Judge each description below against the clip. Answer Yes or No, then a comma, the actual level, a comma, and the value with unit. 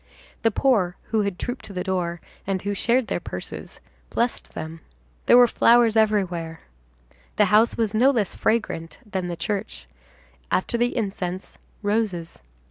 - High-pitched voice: Yes, high, 205 Hz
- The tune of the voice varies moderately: Yes, average, 4.2 semitones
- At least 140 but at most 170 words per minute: Yes, average, 150 wpm